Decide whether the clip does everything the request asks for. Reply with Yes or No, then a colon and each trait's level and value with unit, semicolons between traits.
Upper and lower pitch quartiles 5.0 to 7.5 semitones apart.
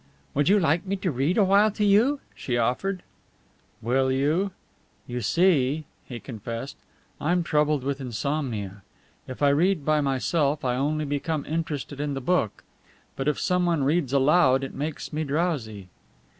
No: average, 4.5 semitones